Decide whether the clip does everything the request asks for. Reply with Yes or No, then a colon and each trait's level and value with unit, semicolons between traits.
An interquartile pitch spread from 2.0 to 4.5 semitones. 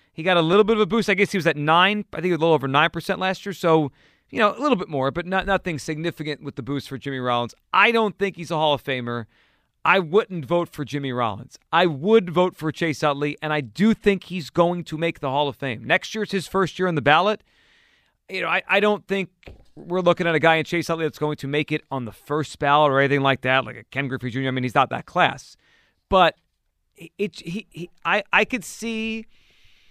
No: average, 5.1 semitones